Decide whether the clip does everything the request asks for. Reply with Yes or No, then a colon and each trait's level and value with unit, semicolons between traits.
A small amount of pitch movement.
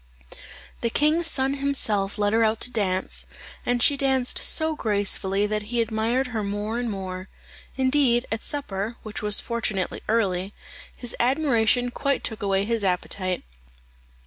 No: average, 3.8 semitones